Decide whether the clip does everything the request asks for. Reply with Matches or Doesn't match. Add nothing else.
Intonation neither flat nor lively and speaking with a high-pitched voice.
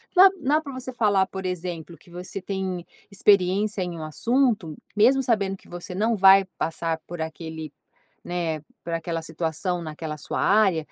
Doesn't match